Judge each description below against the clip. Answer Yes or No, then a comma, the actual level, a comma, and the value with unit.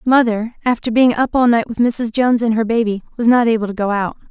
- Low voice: No, high, 230 Hz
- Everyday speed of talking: No, fast, 250 wpm